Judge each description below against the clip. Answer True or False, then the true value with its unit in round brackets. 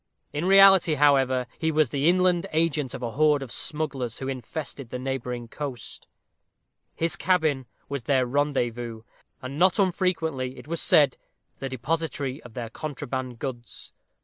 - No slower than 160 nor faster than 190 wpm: False (150 wpm)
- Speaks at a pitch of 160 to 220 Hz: False (140 Hz)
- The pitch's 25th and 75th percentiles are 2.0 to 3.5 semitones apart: False (4.0 semitones)